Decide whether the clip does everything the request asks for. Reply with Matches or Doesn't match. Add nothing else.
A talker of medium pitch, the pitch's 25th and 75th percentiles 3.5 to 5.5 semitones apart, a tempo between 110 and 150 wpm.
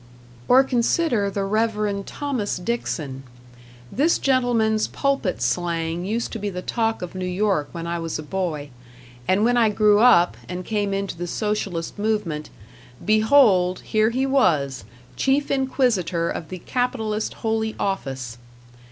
Doesn't match